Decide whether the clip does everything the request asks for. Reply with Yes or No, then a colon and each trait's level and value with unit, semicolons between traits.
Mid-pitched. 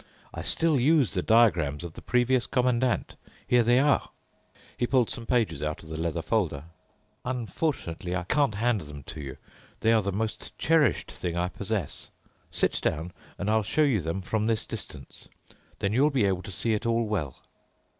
No: low, 110 Hz